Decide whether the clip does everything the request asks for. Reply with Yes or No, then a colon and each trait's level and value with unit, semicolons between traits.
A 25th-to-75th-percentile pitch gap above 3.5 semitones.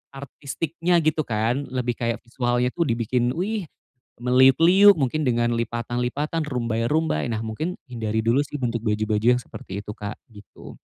Yes: average, 4.3 semitones